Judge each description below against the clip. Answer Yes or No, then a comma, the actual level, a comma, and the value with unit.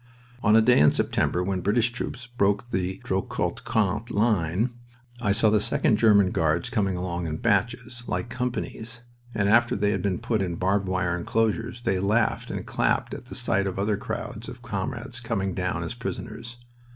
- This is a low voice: Yes, low, 105 Hz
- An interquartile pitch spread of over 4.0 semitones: No, average, 3.7 semitones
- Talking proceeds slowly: No, average, 180 wpm